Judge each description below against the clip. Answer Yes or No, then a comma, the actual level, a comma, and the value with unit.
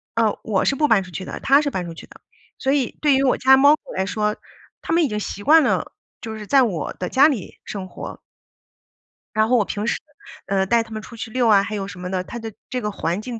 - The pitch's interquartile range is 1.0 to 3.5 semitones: No, average, 5.1 semitones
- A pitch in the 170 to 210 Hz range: No, high, 220 Hz